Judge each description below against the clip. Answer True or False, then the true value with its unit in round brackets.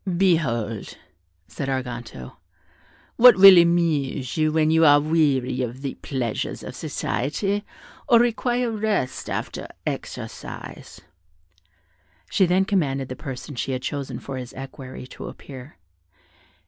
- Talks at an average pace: False (120 wpm)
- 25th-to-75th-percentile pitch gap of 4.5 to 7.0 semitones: True (5.3 semitones)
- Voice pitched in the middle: True (145 Hz)